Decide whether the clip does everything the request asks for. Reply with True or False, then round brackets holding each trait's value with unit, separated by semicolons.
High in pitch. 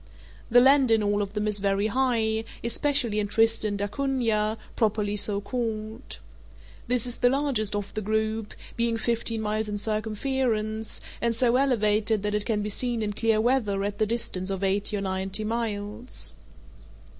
True (220 Hz)